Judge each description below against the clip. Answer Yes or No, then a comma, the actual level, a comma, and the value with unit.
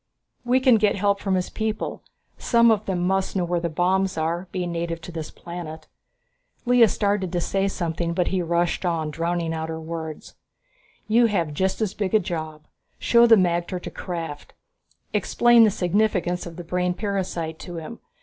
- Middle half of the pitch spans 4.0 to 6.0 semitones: No, average, 3.2 semitones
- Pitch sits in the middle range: Yes, medium, 180 Hz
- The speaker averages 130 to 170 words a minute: No, average, 180 wpm